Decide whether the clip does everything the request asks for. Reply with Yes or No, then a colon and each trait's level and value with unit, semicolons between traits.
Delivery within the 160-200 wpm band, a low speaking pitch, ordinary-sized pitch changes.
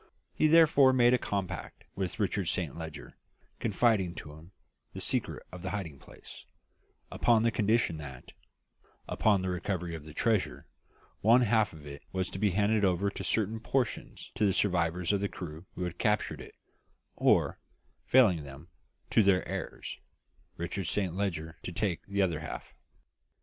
Yes: average, 165 wpm; very low, 95 Hz; average, 4.2 semitones